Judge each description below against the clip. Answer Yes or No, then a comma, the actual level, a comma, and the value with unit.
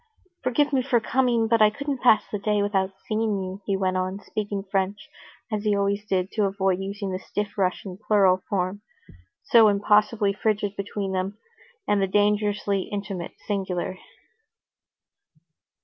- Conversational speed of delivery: Yes, average, 150 wpm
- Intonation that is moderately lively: No, narrow, 1.7 semitones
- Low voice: No, high, 205 Hz